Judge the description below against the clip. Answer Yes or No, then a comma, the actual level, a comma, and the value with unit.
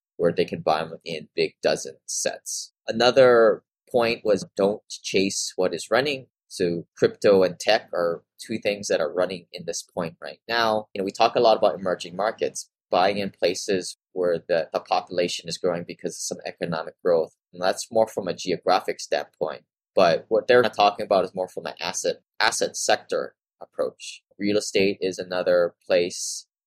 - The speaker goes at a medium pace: Yes, average, 180 wpm